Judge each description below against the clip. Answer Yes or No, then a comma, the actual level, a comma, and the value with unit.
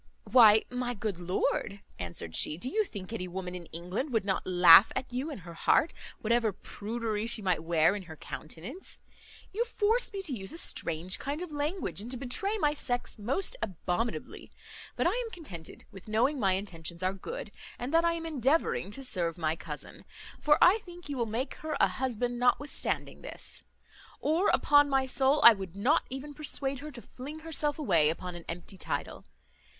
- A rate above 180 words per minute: Yes, average, 190 wpm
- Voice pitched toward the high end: Yes, high, 240 Hz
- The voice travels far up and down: Yes, wide, 8.0 semitones